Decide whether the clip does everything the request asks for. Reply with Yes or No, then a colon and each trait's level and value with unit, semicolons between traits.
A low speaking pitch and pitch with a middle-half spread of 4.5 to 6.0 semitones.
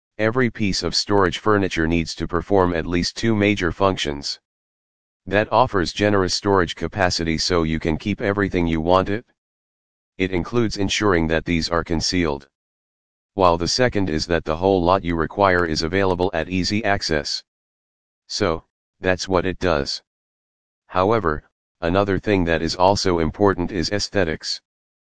No: very low, 90 Hz; average, 3.2 semitones